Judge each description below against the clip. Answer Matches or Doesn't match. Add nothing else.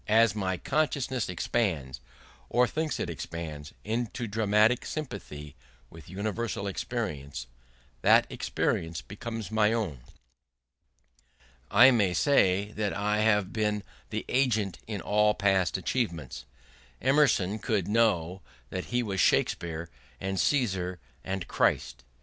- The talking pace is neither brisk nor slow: Doesn't match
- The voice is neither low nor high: Doesn't match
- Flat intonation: Doesn't match